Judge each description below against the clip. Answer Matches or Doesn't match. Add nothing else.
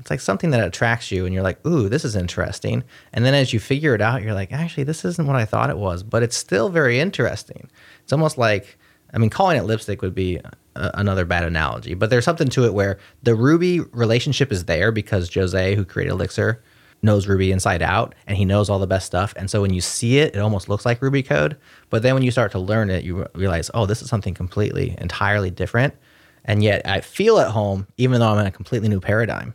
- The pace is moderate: Doesn't match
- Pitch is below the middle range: Matches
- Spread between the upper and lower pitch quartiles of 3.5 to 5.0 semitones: Matches